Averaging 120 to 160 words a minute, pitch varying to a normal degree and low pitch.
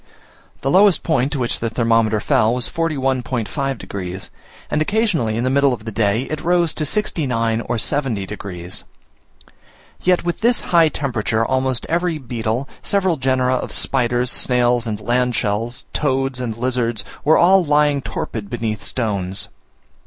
Yes: average, 155 wpm; average, 4.6 semitones; low, 125 Hz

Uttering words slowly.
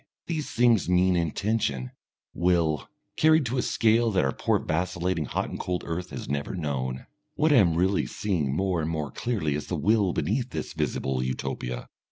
No: average, 180 wpm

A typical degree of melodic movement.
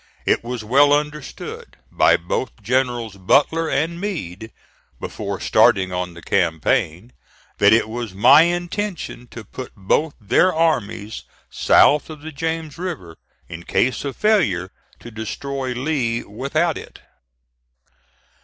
No: wide, 6.9 semitones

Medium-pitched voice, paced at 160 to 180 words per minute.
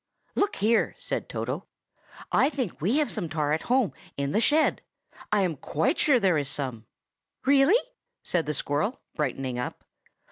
Yes: medium, 180 Hz; average, 165 wpm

